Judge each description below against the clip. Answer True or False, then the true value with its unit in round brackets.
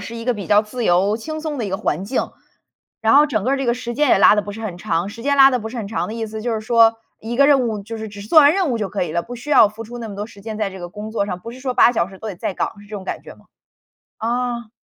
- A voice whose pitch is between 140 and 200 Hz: False (220 Hz)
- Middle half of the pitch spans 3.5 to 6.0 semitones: False (3.1 semitones)